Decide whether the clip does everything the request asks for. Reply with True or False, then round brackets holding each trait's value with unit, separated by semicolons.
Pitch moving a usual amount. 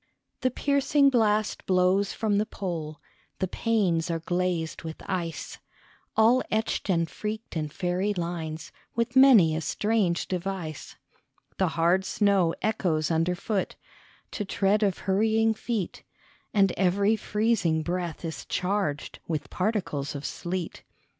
True (4.3 semitones)